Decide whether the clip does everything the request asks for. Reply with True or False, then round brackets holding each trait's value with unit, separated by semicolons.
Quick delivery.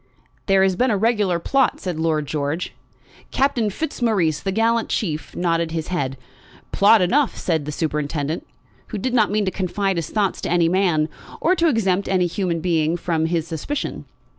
False (175 wpm)